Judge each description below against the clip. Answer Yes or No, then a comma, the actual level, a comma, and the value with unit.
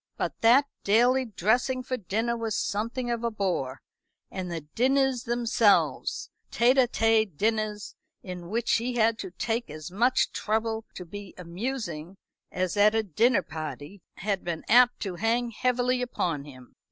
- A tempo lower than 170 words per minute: Yes, average, 155 wpm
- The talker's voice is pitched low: No, high, 220 Hz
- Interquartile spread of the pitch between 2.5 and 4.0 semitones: No, average, 4.6 semitones